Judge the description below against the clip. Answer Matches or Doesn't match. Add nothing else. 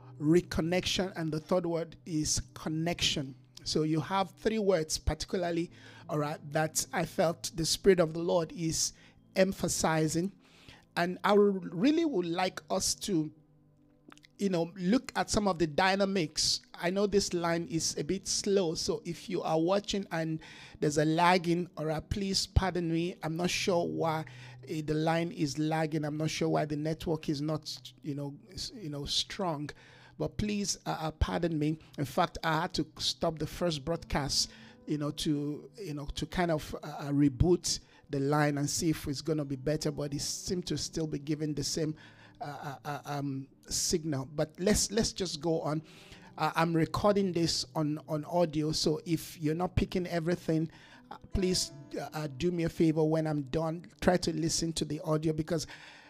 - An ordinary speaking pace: Matches